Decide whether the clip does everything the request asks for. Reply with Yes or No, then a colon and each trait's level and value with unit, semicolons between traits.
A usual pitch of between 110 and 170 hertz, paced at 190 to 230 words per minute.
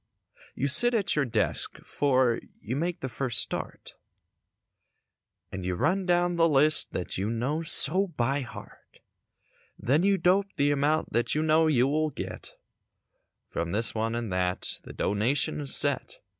No: medium, 140 Hz; average, 155 wpm